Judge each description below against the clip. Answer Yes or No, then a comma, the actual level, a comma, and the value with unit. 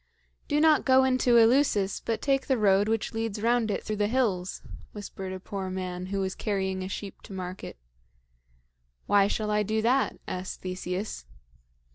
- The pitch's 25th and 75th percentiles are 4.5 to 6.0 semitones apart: No, average, 3.6 semitones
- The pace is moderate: Yes, average, 170 wpm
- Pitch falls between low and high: No, high, 205 Hz